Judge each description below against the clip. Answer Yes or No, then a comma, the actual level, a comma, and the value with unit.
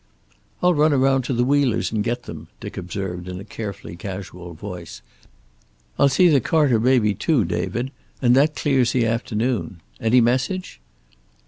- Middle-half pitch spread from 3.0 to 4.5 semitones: No, average, 5.1 semitones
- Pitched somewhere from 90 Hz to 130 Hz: Yes, low, 120 Hz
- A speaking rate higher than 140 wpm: Yes, average, 155 wpm